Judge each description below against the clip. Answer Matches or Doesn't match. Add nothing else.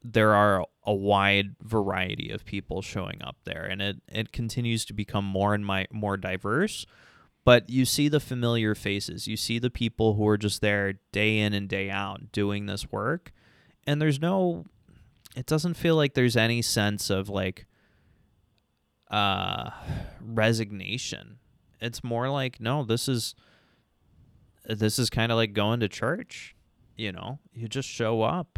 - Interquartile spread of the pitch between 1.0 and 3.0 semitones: Doesn't match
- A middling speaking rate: Matches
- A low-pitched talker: Matches